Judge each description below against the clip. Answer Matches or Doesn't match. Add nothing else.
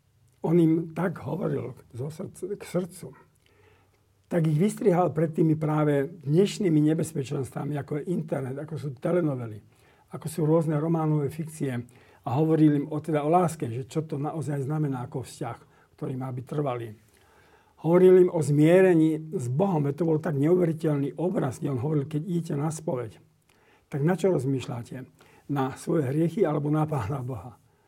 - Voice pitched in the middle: Matches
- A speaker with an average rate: Matches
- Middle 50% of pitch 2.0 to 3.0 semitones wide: Doesn't match